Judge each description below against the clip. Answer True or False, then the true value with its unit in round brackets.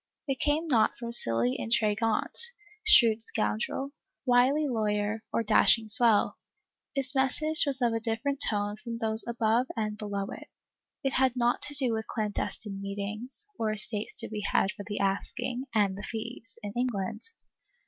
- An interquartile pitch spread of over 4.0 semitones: False (3.4 semitones)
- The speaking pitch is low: False (225 Hz)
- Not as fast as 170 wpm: True (160 wpm)